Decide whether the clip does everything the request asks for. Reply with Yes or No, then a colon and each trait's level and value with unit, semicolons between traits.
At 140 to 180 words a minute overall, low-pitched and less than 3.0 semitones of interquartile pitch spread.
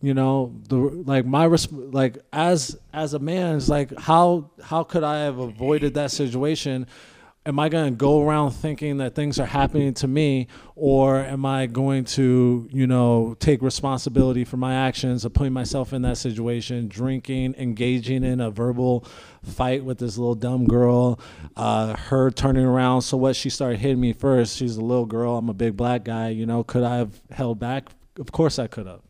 No: average, 190 wpm; low, 130 Hz; narrow, 2.4 semitones